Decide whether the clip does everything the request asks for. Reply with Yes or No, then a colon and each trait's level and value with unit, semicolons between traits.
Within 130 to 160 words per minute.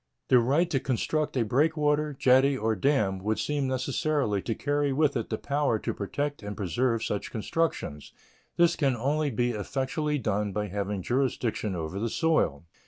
No: average, 170 wpm